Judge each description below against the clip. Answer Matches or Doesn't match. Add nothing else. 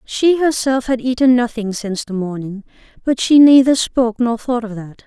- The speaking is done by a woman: Matches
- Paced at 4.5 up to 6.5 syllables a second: Matches